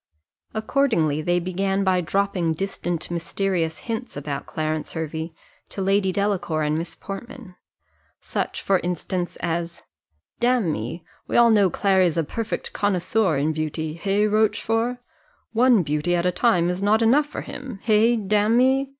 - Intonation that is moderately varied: Yes, average, 4.7 semitones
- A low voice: No, high, 190 Hz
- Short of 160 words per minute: Yes, average, 140 wpm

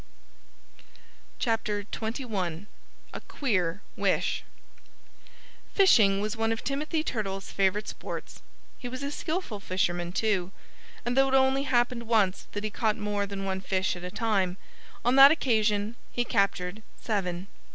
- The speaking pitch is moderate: No, high, 210 Hz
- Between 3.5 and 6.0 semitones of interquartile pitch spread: Yes, average, 4.0 semitones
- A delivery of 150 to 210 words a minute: No, slow, 135 wpm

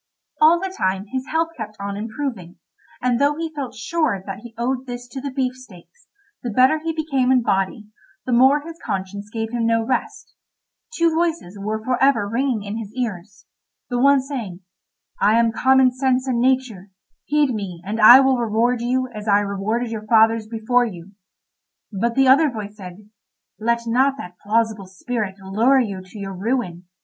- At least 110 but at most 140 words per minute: No, average, 180 wpm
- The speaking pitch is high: Yes, high, 235 Hz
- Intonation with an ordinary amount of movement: Yes, average, 4.3 semitones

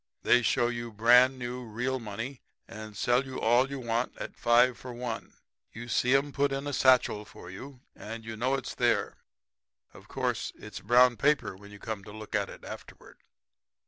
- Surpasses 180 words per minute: Yes, average, 190 wpm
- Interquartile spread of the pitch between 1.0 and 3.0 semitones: Yes, narrow, 2.5 semitones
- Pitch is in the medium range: No, low, 120 Hz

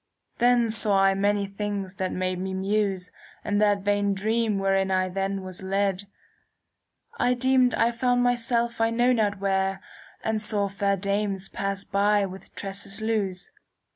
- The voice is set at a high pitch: Yes, high, 200 Hz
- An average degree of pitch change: No, narrow, 2.3 semitones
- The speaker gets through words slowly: No, average, 165 wpm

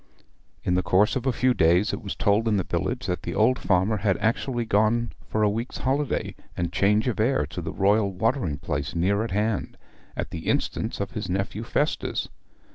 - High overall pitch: No, low, 105 Hz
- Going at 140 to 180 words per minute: No, average, 200 wpm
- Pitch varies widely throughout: No, average, 4.0 semitones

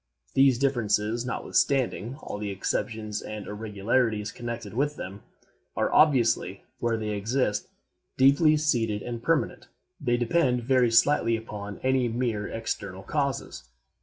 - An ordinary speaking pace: No, slow, 125 wpm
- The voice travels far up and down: No, average, 3.8 semitones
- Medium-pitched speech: No, low, 115 Hz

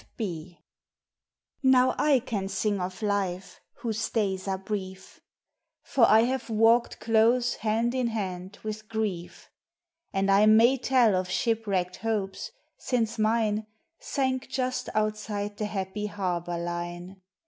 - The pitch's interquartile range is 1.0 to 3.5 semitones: Yes, average, 3.2 semitones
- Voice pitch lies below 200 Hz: No, high, 215 Hz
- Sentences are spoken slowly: Yes, slow, 130 wpm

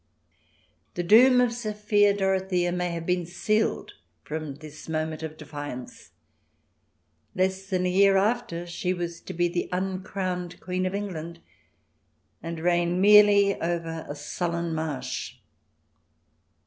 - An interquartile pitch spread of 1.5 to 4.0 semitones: Yes, average, 2.7 semitones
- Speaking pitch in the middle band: Yes, medium, 180 Hz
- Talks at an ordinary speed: No, slow, 125 wpm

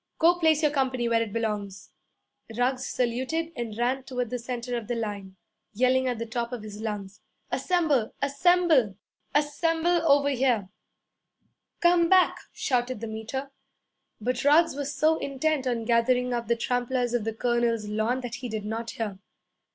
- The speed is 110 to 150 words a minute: No, average, 160 wpm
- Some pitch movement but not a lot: Yes, average, 3.6 semitones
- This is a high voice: Yes, high, 245 Hz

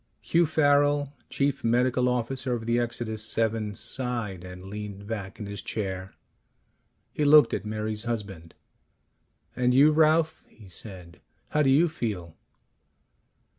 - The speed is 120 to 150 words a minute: Yes, slow, 135 wpm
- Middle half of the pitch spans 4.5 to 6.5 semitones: Yes, average, 5.2 semitones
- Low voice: Yes, low, 115 Hz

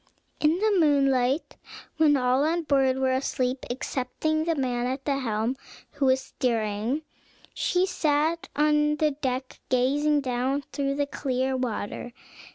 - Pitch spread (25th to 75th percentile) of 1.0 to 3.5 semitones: Yes, average, 2.8 semitones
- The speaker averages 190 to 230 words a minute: No, average, 140 wpm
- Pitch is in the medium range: No, very high, 275 Hz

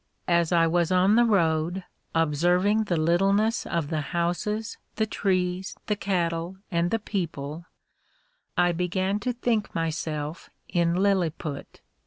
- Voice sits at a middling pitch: Yes, medium, 175 Hz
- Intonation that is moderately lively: Yes, average, 3.2 semitones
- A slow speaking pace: Yes, slow, 130 wpm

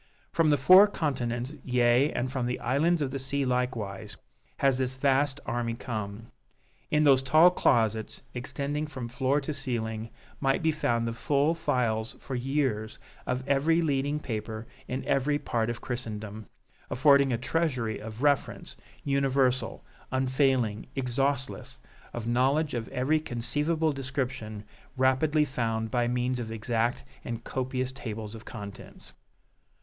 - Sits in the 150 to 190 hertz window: No, low, 130 Hz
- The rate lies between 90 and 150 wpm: Yes, average, 140 wpm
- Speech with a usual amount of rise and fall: Yes, average, 3.2 semitones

